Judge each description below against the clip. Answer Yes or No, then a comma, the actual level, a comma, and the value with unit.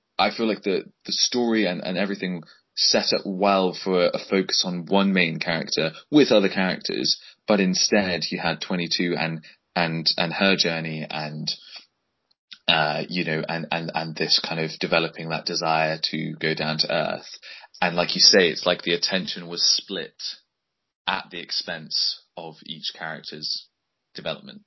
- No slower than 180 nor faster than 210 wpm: No, average, 165 wpm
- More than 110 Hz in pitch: No, very low, 85 Hz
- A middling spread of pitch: Yes, average, 3.0 semitones